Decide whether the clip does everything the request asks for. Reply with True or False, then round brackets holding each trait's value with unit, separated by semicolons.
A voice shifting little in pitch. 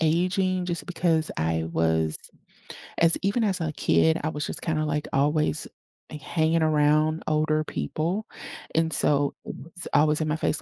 True (2.0 semitones)